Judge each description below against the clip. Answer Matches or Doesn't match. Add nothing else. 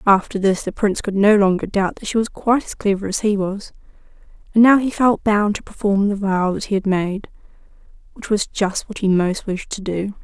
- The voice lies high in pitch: Matches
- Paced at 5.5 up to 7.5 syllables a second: Doesn't match